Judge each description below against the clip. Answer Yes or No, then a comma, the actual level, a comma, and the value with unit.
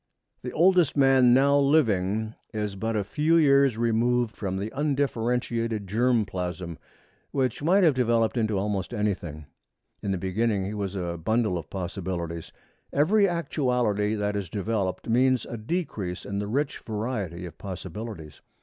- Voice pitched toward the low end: Yes, low, 110 Hz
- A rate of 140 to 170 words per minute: Yes, average, 150 wpm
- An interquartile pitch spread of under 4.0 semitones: No, average, 5.1 semitones